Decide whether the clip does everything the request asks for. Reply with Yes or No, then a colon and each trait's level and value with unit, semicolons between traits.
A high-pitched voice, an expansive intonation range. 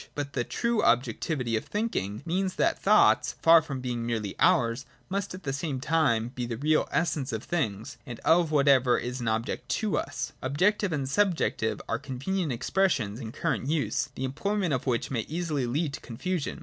No: medium, 140 Hz; wide, 5.8 semitones